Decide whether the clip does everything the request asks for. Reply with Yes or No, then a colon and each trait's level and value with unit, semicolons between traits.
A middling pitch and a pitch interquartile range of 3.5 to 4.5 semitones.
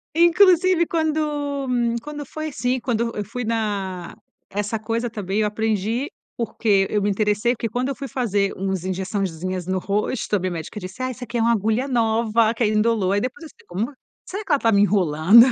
No: high, 225 Hz; average, 4.2 semitones